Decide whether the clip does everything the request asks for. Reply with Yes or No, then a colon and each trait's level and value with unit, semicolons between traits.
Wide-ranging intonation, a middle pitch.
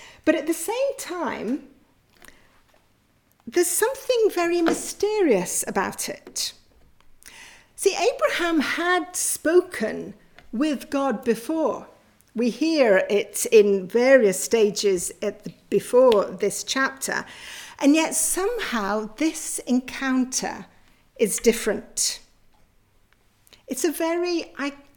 No: wide, 8.2 semitones; very high, 280 Hz